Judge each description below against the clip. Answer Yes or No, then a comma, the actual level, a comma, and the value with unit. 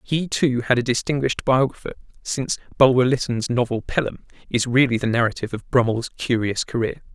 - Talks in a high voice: No, low, 125 Hz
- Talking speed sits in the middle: Yes, average, 160 wpm